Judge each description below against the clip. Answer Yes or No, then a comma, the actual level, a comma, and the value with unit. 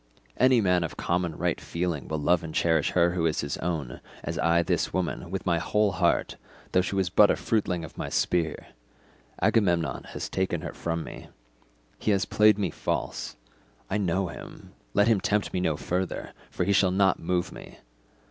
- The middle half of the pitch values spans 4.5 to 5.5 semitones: No, narrow, 2.5 semitones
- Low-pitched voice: Yes, very low, 90 Hz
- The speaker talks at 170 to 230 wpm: Yes, average, 190 wpm